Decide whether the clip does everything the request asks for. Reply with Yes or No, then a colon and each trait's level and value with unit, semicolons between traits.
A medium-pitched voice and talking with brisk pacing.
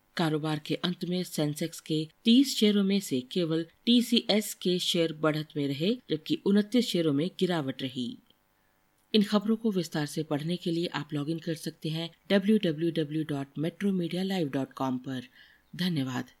No: medium, 165 Hz; average, 145 wpm